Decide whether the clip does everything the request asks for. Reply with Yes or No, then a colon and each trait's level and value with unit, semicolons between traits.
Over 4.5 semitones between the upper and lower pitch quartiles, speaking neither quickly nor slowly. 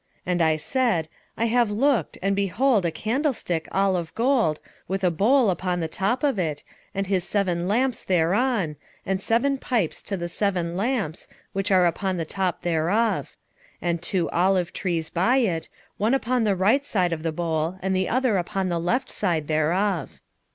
Yes: average, 4.9 semitones; average, 180 wpm